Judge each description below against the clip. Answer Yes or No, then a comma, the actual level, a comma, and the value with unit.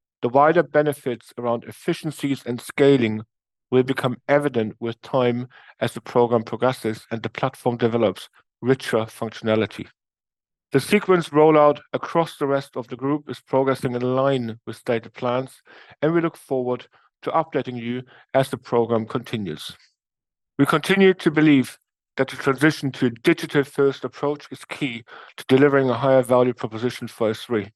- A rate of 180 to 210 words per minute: No, average, 155 wpm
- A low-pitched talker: Yes, low, 130 Hz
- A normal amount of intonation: Yes, average, 3.5 semitones